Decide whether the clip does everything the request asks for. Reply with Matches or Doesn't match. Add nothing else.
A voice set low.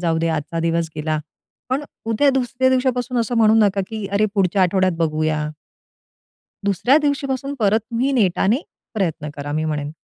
Doesn't match